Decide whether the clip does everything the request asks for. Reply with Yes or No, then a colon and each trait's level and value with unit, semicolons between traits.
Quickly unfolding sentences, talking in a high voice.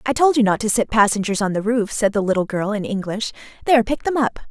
Yes: fast, 265 wpm; high, 220 Hz